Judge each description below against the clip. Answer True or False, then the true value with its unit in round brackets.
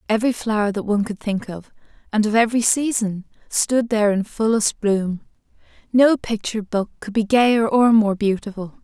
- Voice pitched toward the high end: True (215 Hz)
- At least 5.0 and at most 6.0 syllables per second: True (5.2 syllables/s)